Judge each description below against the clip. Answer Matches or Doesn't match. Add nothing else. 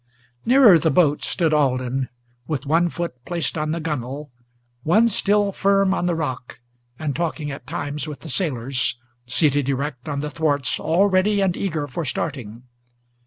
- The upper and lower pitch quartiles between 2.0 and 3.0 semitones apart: Doesn't match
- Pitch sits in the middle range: Matches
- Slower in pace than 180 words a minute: Matches